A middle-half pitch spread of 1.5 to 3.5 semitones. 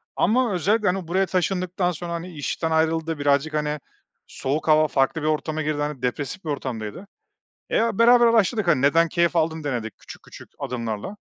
No: average, 4.0 semitones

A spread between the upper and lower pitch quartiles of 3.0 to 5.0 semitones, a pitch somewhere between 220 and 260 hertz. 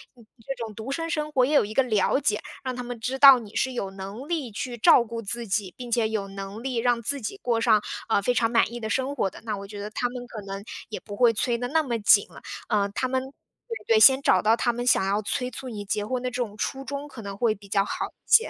Yes: average, 3.5 semitones; high, 235 Hz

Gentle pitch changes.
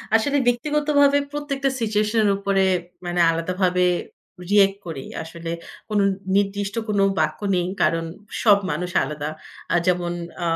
No: average, 4.4 semitones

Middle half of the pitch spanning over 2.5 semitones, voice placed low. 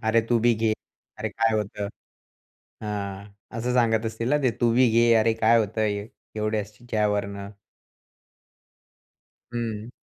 No: narrow, 1.9 semitones; low, 110 Hz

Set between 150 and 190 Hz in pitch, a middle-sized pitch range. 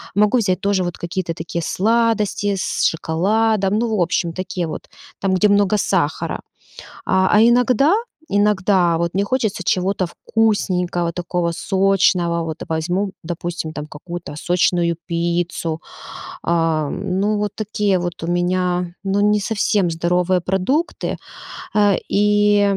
Yes: medium, 185 Hz; average, 3.1 semitones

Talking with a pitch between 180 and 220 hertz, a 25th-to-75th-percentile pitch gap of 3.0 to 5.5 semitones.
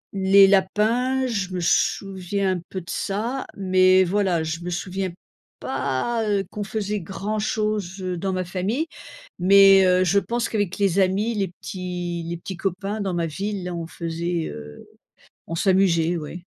No: high, 190 Hz; narrow, 2.5 semitones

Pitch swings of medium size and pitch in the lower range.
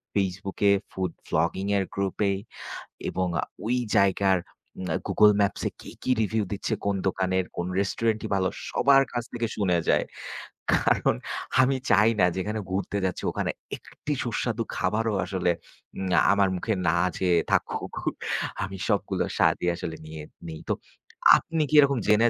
Yes: average, 3.0 semitones; low, 100 Hz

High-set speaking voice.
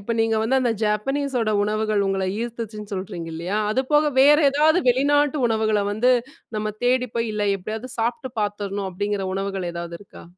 Yes: high, 220 Hz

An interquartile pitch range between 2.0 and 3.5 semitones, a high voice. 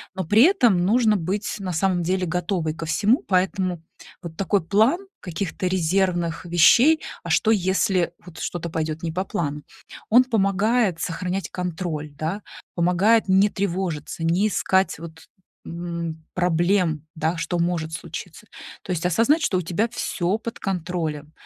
No: average, 3.2 semitones; medium, 180 Hz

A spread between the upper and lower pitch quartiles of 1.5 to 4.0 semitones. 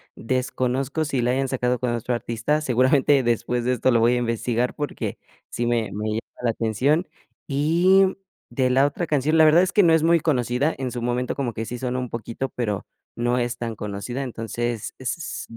Yes: average, 3.1 semitones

